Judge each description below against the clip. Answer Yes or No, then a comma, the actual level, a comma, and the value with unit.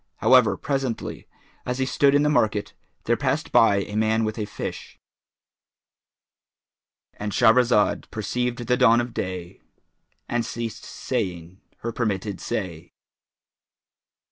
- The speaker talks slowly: Yes, slow, 115 wpm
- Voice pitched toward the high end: No, low, 115 Hz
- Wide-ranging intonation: No, average, 3.2 semitones